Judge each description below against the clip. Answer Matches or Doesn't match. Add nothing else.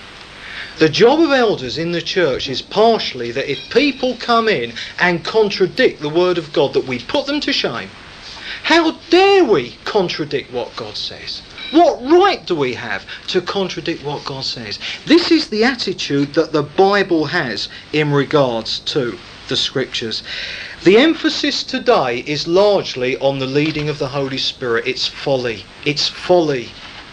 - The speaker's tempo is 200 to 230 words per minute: Doesn't match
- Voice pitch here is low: Doesn't match